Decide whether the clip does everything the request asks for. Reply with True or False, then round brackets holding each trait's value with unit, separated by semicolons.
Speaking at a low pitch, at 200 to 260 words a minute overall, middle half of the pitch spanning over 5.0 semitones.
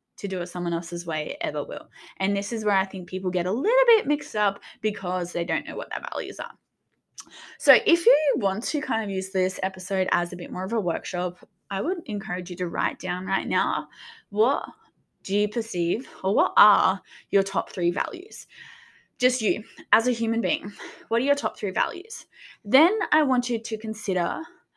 False (205 Hz; 205 wpm; 5.6 semitones)